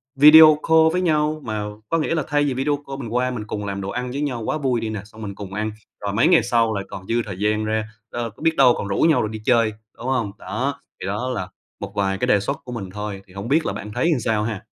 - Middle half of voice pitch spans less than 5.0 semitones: No, average, 5.3 semitones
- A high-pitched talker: No, low, 115 Hz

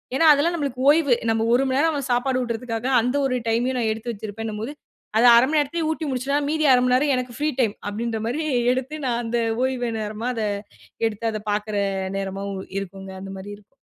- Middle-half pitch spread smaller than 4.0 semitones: Yes, average, 3.6 semitones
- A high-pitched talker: Yes, high, 245 Hz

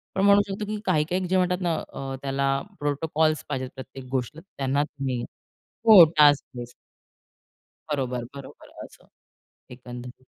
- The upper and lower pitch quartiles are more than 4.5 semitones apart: Yes, average, 4.9 semitones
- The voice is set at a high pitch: No, medium, 145 Hz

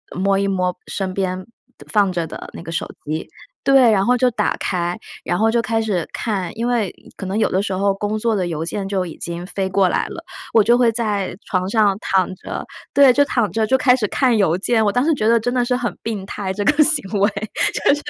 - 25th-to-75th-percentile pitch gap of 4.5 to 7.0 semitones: No, average, 3.9 semitones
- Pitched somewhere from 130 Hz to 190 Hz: No, high, 205 Hz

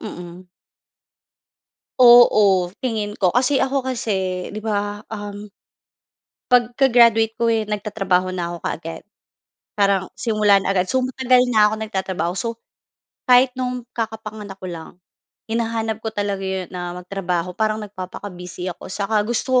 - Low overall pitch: No, high, 210 Hz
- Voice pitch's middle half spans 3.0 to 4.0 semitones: Yes, average, 3.6 semitones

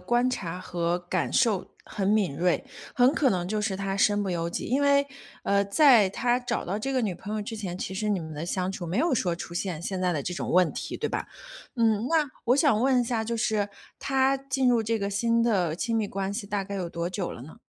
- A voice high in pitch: Yes, high, 205 Hz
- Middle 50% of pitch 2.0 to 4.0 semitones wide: No, average, 4.8 semitones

